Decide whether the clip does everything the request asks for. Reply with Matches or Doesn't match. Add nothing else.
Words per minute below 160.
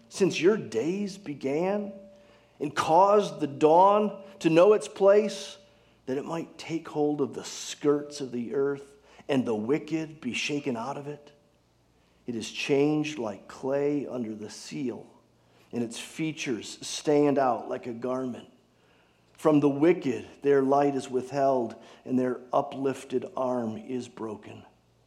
Matches